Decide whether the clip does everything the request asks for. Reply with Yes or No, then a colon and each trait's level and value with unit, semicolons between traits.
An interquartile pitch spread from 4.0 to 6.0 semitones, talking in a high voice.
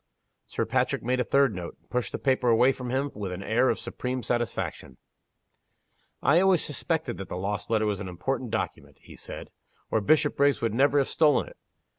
No: average, 4.8 semitones; low, 125 Hz